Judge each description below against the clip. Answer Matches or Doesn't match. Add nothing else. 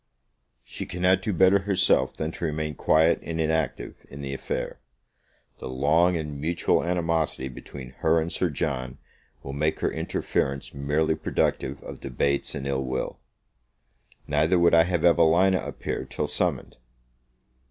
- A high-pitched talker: Doesn't match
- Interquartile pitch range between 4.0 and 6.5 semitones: Doesn't match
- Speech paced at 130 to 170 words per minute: Matches